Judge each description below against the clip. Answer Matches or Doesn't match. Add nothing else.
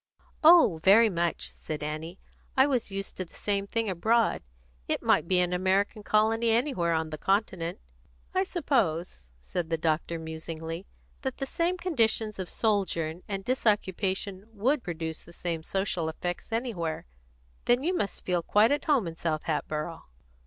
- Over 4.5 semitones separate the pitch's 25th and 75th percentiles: Matches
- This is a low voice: Doesn't match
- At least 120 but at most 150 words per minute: Doesn't match